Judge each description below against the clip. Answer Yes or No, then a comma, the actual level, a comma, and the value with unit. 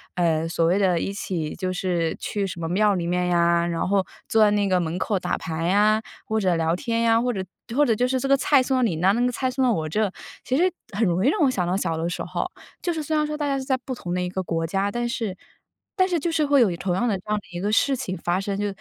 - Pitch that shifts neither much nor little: No, wide, 6.0 semitones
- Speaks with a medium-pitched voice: No, high, 200 Hz